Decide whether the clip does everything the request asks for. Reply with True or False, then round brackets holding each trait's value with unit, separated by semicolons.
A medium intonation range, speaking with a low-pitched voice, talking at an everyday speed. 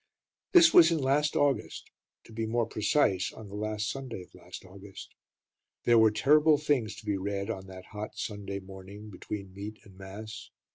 True (3.4 semitones; 105 Hz; 180 wpm)